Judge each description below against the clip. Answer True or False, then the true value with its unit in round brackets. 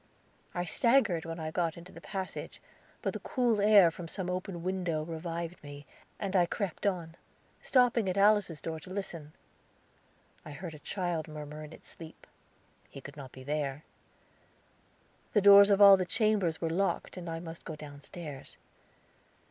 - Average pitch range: True (3.8 semitones)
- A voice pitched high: False (170 Hz)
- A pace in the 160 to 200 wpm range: True (165 wpm)